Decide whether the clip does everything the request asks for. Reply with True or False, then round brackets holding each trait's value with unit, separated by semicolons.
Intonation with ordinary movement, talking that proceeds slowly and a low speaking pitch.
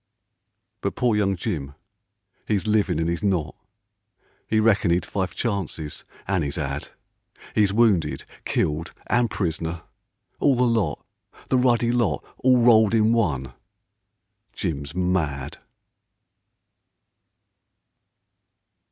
False (6.0 semitones; 110 wpm; 95 Hz)